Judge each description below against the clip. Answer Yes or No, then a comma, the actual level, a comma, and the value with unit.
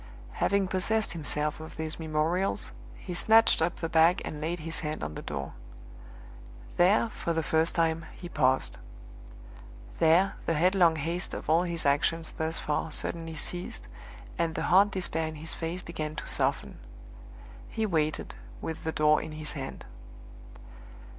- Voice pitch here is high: No, medium, 165 Hz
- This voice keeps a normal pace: Yes, average, 155 wpm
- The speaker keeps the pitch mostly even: Yes, narrow, 2.2 semitones